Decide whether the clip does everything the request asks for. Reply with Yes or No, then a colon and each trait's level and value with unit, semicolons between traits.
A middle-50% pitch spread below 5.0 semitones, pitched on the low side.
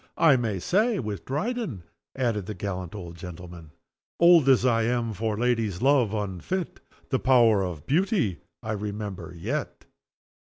No: wide, 5.6 semitones; low, 110 Hz